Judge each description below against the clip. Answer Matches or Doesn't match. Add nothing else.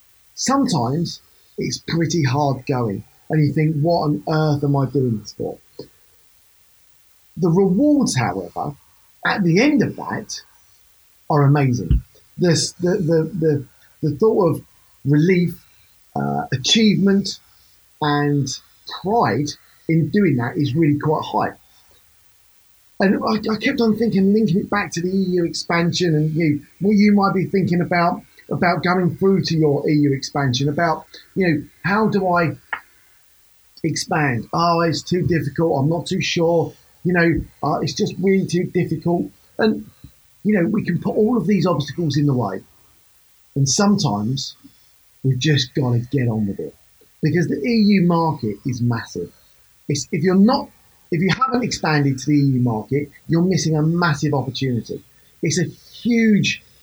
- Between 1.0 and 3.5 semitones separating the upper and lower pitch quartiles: Doesn't match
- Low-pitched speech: Doesn't match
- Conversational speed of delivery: Matches